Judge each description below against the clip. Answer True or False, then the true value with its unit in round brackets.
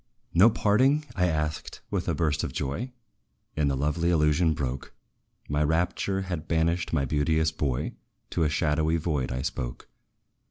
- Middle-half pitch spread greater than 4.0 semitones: False (3.0 semitones)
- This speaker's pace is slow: False (155 wpm)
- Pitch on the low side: True (80 Hz)